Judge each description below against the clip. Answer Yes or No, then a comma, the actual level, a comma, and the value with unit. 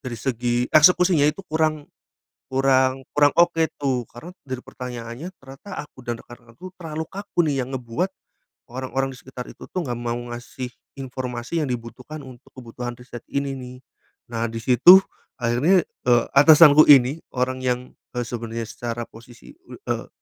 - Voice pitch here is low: Yes, low, 130 Hz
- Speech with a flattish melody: No, average, 3.6 semitones